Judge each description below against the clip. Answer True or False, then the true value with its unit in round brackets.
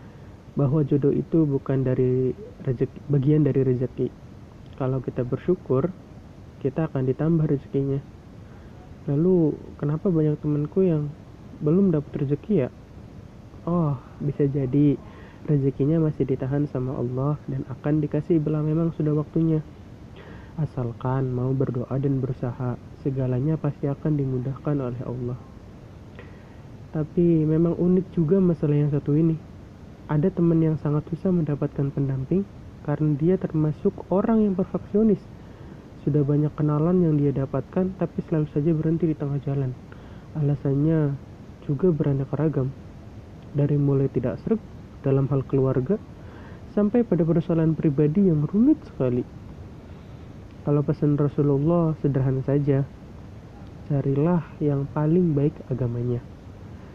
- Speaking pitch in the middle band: True (145 Hz)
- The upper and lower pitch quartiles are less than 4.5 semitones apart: True (3.7 semitones)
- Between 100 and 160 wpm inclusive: True (120 wpm)